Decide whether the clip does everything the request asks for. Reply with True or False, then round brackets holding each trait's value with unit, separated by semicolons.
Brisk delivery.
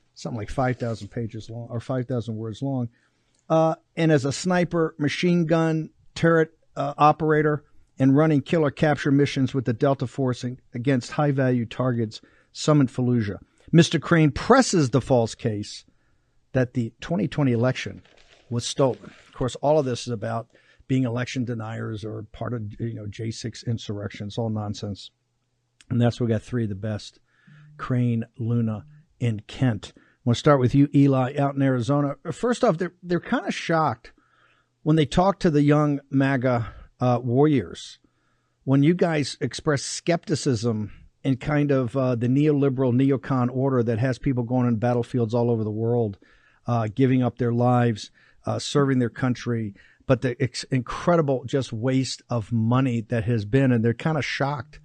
False (170 wpm)